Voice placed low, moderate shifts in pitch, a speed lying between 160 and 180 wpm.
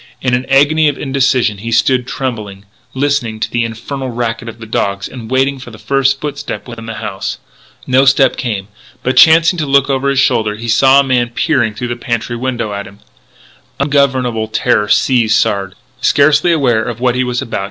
Yes: low, 125 Hz; average, 3.3 semitones; average, 170 wpm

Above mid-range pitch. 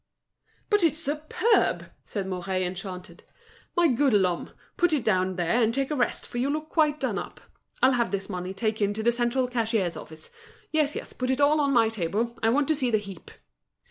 Yes: high, 235 Hz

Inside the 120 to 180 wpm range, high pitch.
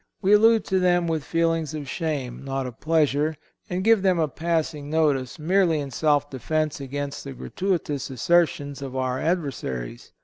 No: average, 165 wpm; medium, 155 Hz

